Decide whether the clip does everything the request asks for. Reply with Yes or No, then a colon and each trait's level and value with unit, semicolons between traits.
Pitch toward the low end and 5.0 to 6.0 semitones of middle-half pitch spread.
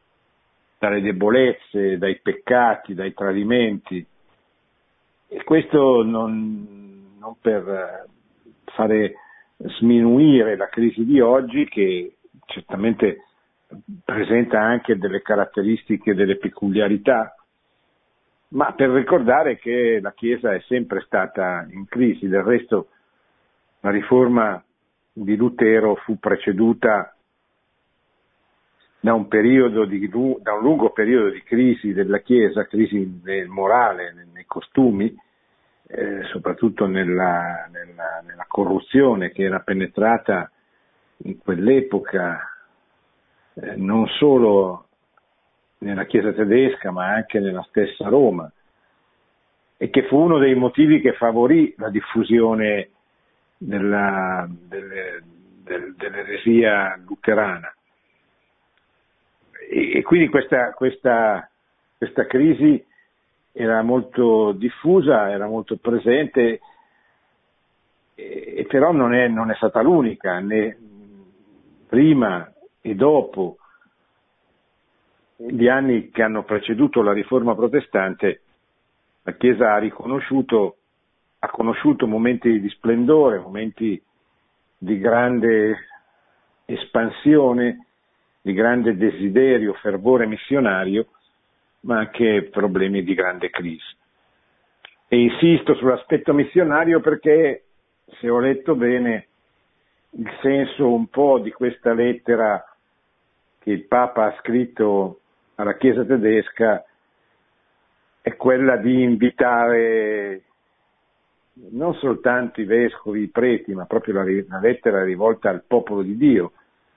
No: low, 115 Hz; average, 3.5 semitones